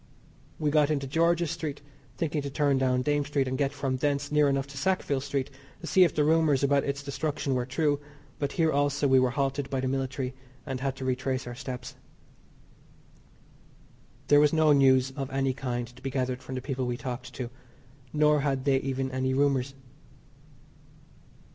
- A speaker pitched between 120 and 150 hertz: Yes, low, 135 Hz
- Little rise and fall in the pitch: Yes, narrow, 1.9 semitones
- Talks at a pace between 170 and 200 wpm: Yes, average, 185 wpm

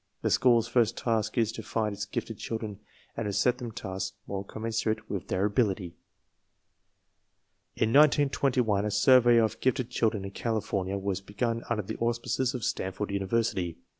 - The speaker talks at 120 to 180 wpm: Yes, average, 165 wpm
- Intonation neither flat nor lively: Yes, average, 3.0 semitones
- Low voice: Yes, low, 110 Hz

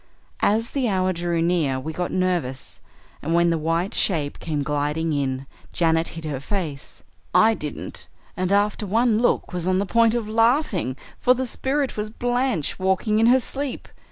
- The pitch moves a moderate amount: No, wide, 5.8 semitones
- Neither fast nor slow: Yes, average, 175 wpm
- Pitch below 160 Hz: No, medium, 185 Hz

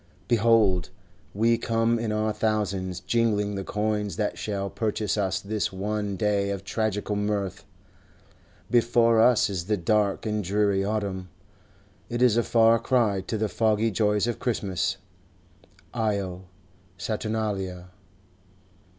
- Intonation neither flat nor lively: No, narrow, 2.2 semitones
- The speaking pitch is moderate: No, low, 105 Hz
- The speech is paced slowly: Yes, slow, 125 wpm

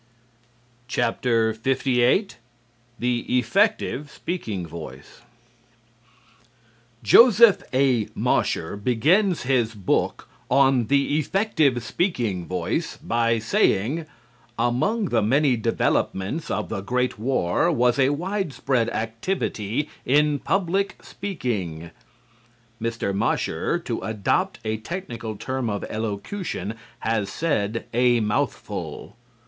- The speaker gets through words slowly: Yes, slow, 95 wpm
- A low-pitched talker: Yes, low, 120 Hz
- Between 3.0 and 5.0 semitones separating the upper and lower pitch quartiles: No, wide, 5.5 semitones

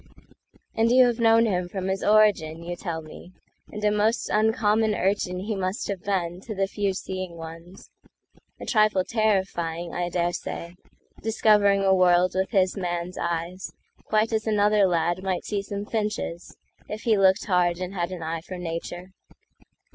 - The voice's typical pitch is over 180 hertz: Yes, high, 190 Hz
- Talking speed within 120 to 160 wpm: Yes, average, 150 wpm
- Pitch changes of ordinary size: Yes, average, 3.2 semitones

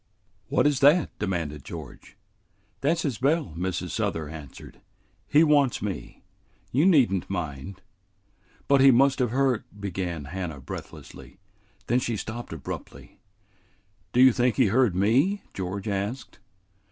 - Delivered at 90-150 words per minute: Yes, average, 140 wpm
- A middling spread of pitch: No, wide, 6.8 semitones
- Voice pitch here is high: No, low, 110 Hz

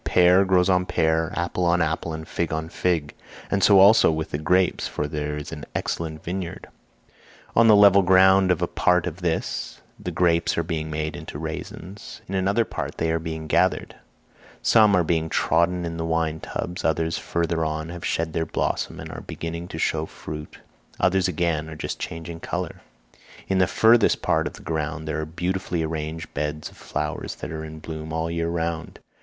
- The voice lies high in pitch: No, very low, 85 Hz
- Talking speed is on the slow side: No, average, 195 wpm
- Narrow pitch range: Yes, narrow, 2.3 semitones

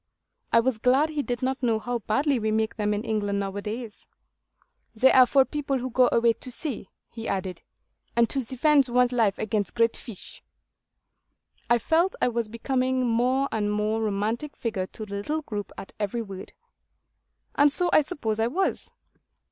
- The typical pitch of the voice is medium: No, high, 235 Hz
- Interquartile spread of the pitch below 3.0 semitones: No, average, 3.5 semitones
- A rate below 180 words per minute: No, average, 185 wpm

